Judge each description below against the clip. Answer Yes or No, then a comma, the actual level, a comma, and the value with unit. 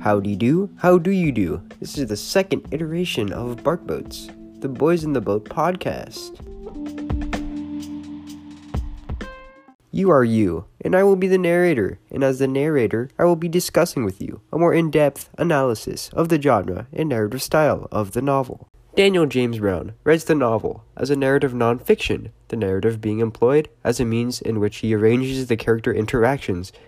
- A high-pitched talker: No, low, 130 Hz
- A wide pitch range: Yes, wide, 7.2 semitones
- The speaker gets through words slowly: No, average, 175 wpm